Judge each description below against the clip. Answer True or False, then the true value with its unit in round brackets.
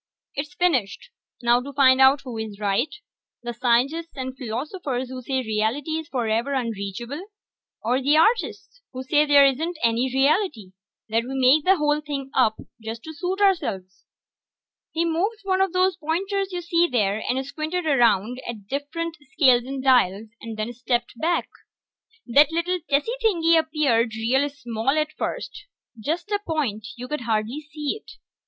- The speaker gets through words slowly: False (160 wpm)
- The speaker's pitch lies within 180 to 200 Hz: False (270 Hz)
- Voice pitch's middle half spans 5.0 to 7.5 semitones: True (5.4 semitones)